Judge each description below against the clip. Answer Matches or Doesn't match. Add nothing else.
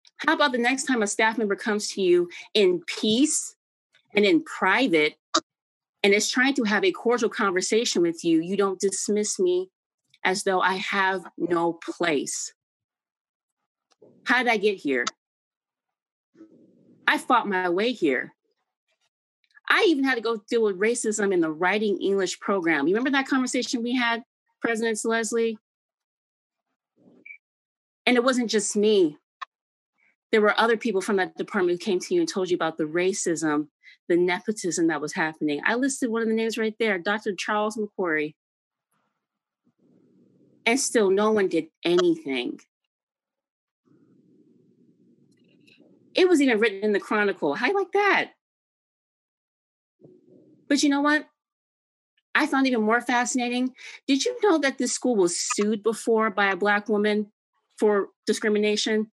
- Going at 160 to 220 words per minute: Doesn't match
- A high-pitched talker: Matches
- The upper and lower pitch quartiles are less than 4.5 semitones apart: Doesn't match